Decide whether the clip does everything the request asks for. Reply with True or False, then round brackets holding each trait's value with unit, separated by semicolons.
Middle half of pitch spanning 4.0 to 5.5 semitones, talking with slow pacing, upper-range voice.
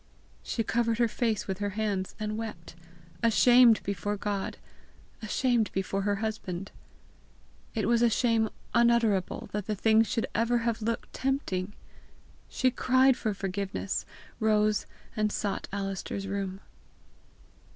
False (2.7 semitones; 130 wpm; 215 Hz)